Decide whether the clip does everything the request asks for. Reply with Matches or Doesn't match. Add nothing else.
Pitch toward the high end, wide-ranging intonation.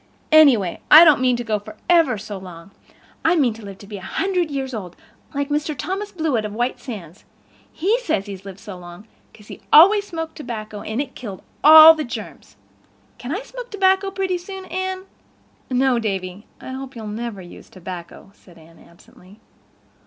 Matches